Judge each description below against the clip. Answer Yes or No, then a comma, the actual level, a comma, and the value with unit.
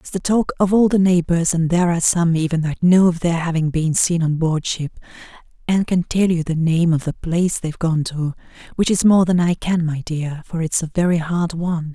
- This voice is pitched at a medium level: Yes, medium, 170 Hz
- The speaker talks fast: Yes, fast, 240 wpm